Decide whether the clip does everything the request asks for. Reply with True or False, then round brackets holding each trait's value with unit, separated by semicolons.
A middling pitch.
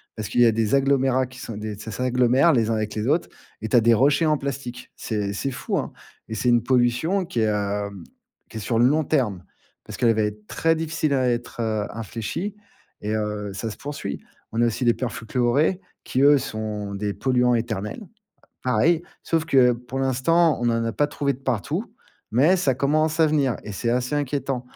False (125 Hz)